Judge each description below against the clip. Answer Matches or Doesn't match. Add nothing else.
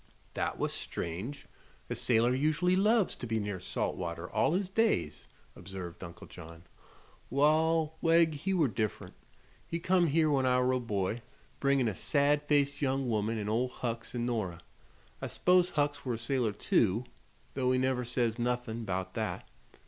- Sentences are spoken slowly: Doesn't match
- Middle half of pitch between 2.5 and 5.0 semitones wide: Doesn't match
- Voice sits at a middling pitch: Doesn't match